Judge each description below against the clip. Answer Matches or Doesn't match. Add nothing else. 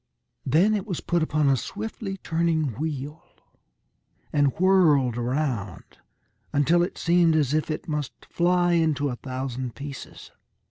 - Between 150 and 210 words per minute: Doesn't match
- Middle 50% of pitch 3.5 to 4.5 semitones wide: Matches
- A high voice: Doesn't match